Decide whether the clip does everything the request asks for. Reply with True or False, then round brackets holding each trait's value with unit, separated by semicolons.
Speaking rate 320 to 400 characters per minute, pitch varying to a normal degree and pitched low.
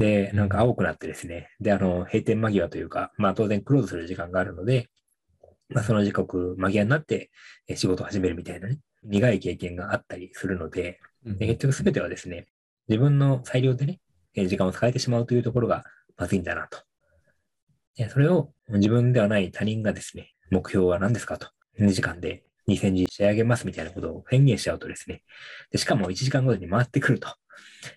True (390 characters per minute; 4.7 semitones; 105 Hz)